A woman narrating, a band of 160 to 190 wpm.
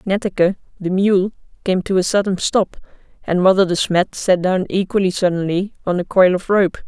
Yes: female; average, 185 wpm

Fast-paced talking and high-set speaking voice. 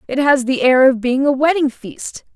Yes: fast, 230 wpm; very high, 275 Hz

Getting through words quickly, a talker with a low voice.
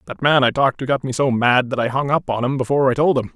Yes: fast, 340 wpm; low, 130 Hz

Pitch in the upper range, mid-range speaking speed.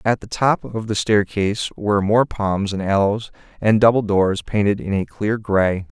No: low, 105 Hz; average, 190 wpm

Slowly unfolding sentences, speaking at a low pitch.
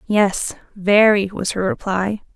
No: slow, 130 wpm; high, 200 Hz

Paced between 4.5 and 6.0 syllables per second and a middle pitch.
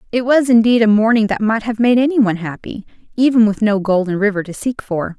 No: 5.8 syllables/s; high, 220 Hz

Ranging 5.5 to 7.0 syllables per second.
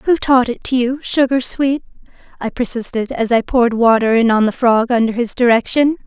No: 5.2 syllables/s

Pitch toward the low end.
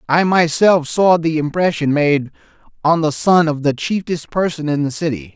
No: medium, 160 Hz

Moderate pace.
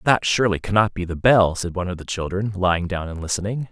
No: fast, 240 wpm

